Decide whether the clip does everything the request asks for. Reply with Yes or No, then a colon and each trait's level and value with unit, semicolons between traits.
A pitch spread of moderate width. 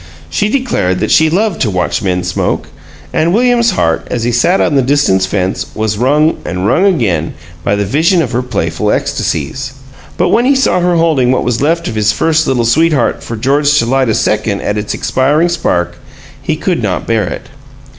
No: wide, 7.9 semitones